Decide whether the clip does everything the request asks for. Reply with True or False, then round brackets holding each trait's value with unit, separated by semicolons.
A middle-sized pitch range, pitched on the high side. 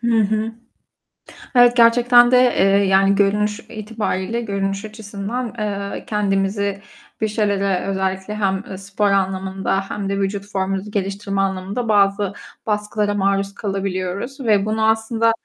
False (1.9 semitones; 200 Hz)